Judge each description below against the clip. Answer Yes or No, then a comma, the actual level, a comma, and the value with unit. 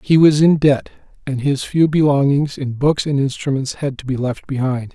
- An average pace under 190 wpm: No, fast, 205 wpm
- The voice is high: No, medium, 140 Hz